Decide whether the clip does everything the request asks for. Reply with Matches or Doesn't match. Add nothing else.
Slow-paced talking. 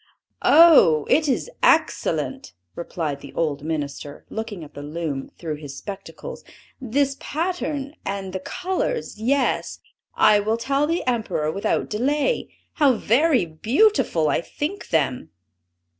Matches